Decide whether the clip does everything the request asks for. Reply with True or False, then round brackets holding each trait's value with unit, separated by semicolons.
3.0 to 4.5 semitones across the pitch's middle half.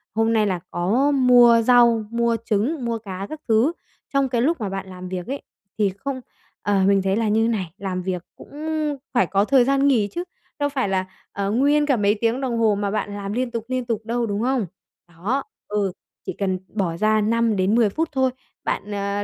True (3.9 semitones)